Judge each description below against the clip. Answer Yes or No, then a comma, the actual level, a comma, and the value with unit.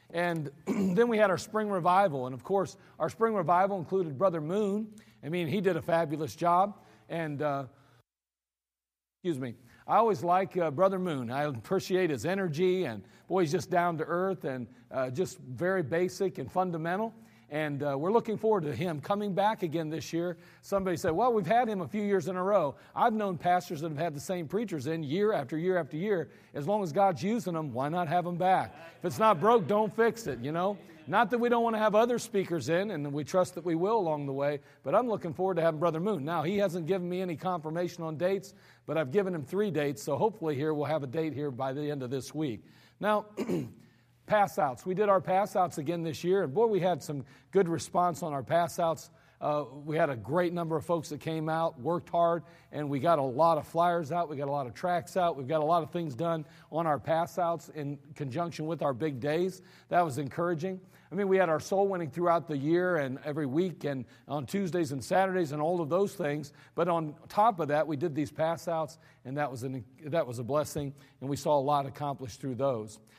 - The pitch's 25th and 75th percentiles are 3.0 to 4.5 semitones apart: Yes, average, 4.1 semitones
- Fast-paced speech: Yes, fast, 230 wpm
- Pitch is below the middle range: No, medium, 170 Hz